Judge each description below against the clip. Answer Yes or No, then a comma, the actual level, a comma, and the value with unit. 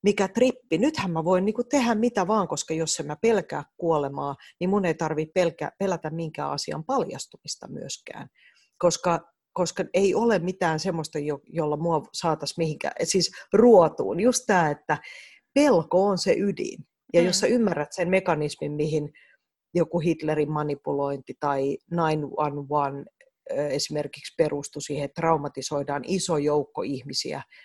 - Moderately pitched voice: Yes, medium, 165 Hz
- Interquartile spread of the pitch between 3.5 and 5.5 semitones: Yes, average, 4.3 semitones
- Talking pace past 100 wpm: Yes, average, 140 wpm